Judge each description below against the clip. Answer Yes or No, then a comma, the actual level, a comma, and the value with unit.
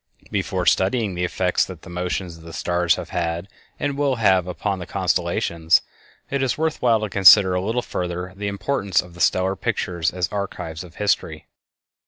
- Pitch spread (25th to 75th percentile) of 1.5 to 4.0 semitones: Yes, average, 2.8 semitones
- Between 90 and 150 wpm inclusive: No, average, 185 wpm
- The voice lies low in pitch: Yes, very low, 95 Hz